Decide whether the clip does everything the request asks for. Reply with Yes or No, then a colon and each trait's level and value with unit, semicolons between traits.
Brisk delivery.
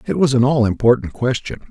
Yes: fast, 210 wpm